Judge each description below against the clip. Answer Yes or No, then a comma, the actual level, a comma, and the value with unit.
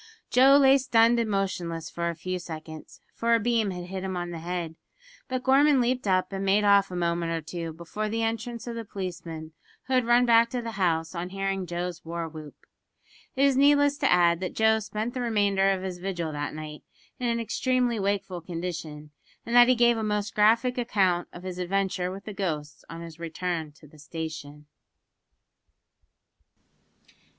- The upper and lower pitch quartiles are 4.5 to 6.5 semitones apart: Yes, average, 5.3 semitones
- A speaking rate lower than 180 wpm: No, average, 190 wpm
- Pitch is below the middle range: No, high, 190 Hz